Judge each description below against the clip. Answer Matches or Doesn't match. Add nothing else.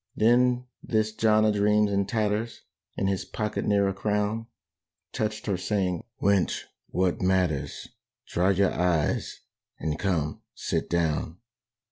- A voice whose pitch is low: Matches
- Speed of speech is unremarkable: Doesn't match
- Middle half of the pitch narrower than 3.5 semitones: Matches